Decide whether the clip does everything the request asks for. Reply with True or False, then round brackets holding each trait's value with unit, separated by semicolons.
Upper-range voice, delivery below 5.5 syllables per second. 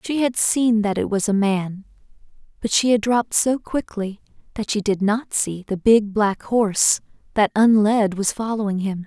True (210 Hz; 4.6 syllables/s)